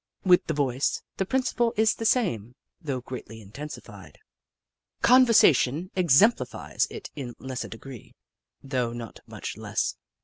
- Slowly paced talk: Yes, slow, 130 wpm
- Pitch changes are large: Yes, wide, 8.2 semitones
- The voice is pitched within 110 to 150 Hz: Yes, medium, 140 Hz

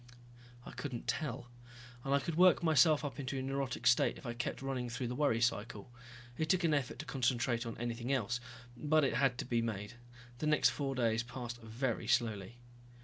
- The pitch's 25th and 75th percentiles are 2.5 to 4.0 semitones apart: Yes, average, 2.9 semitones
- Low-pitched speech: Yes, low, 125 Hz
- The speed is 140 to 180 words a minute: No, average, 195 wpm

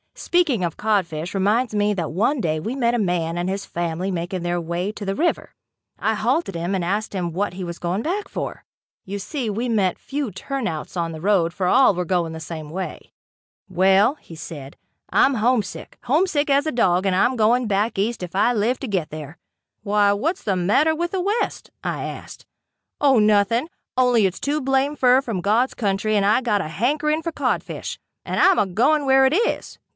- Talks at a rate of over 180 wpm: Yes, average, 200 wpm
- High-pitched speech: Yes, high, 205 Hz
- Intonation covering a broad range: Yes, wide, 6.2 semitones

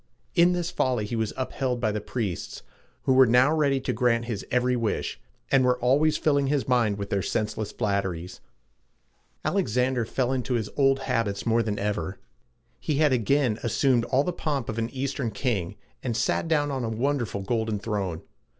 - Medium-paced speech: Yes, average, 180 wpm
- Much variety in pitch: No, average, 4.0 semitones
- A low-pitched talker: Yes, low, 125 Hz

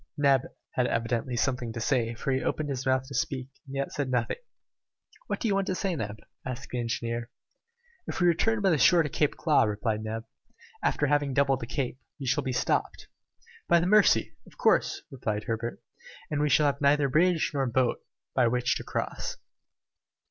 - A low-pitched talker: Yes, low, 130 Hz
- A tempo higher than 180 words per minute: Yes, average, 200 wpm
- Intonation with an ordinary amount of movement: Yes, average, 3.8 semitones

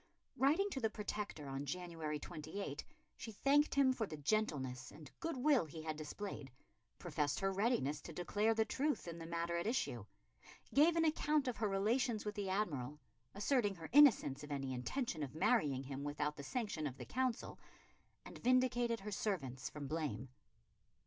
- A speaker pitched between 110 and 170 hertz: No, high, 190 Hz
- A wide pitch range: Yes, wide, 8.3 semitones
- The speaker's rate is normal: Yes, average, 175 wpm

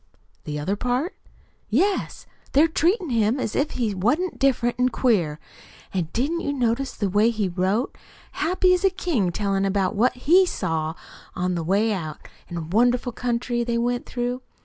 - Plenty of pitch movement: Yes, wide, 5.8 semitones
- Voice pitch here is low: No, high, 235 Hz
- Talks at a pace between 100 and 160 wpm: No, average, 170 wpm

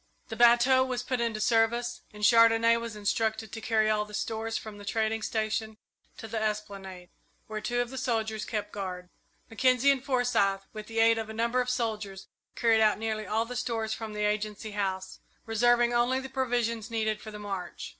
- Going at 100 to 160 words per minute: No, average, 195 wpm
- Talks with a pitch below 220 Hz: No, high, 225 Hz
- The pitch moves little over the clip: Yes, narrow, 2.0 semitones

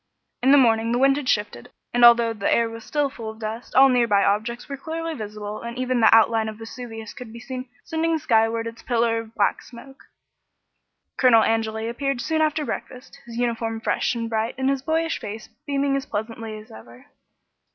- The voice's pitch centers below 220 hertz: No, high, 235 Hz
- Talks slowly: No, average, 200 wpm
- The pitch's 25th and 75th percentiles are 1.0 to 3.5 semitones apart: Yes, average, 3.0 semitones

